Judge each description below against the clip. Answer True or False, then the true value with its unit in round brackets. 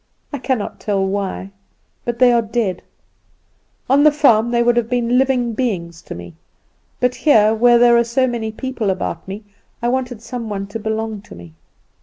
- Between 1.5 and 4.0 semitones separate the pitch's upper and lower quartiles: True (3.2 semitones)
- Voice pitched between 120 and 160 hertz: False (235 Hz)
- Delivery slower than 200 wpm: True (185 wpm)